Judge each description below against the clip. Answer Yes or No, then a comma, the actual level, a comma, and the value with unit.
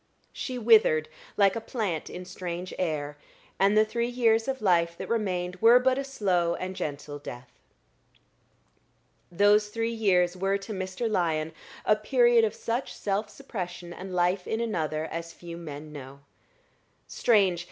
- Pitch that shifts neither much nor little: Yes, average, 4.7 semitones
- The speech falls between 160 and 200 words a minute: No, average, 150 wpm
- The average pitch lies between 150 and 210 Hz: Yes, high, 190 Hz